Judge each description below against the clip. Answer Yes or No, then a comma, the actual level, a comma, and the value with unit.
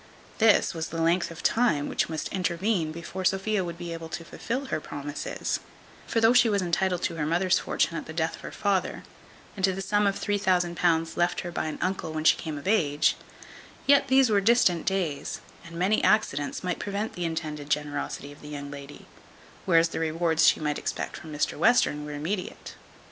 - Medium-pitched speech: Yes, medium, 170 Hz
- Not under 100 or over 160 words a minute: No, average, 200 wpm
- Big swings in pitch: No, average, 3.7 semitones